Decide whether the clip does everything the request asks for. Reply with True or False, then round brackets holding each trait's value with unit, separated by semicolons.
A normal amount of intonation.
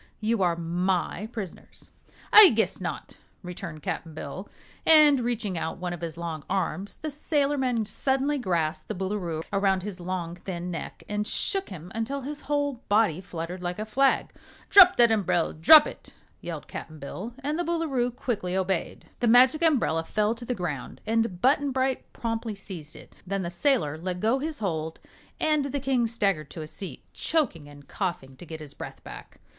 False (7.0 semitones)